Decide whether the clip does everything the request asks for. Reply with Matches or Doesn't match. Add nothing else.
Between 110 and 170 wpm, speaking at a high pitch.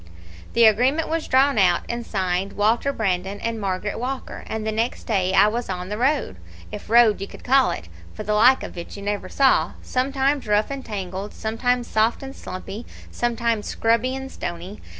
Doesn't match